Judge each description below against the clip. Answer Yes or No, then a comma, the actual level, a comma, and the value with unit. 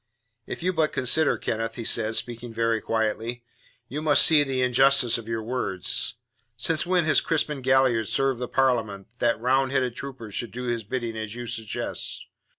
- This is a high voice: No, low, 120 Hz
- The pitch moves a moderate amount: Yes, average, 3.0 semitones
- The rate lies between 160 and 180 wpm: Yes, average, 170 wpm